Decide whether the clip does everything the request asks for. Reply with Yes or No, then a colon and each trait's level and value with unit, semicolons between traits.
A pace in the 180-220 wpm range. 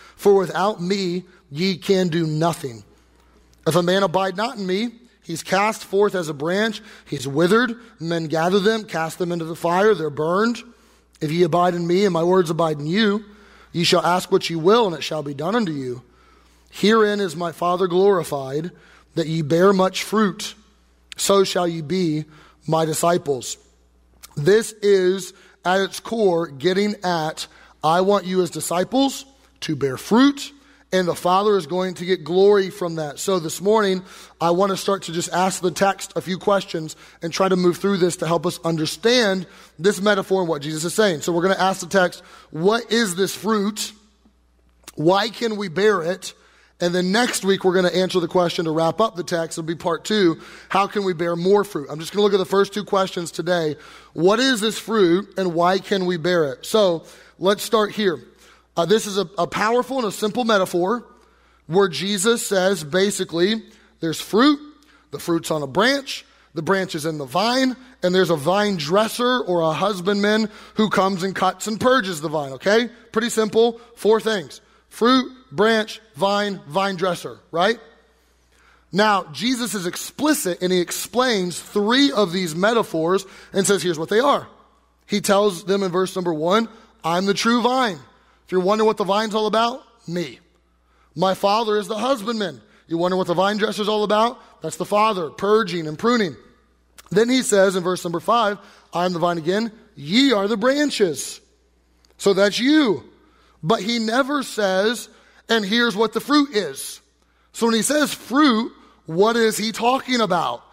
Yes: average, 185 wpm